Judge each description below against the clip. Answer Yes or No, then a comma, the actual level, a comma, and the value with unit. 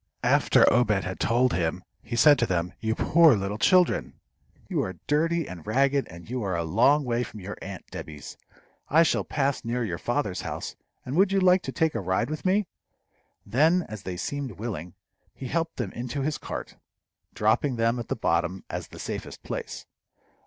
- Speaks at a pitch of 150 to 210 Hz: No, low, 120 Hz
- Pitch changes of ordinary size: No, wide, 7.2 semitones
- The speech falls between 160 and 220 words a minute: Yes, average, 190 wpm